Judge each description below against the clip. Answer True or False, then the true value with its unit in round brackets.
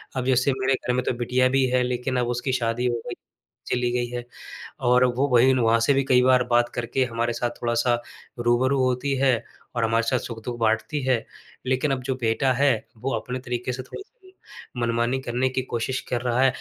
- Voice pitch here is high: False (125 Hz)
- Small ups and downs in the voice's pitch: True (1.5 semitones)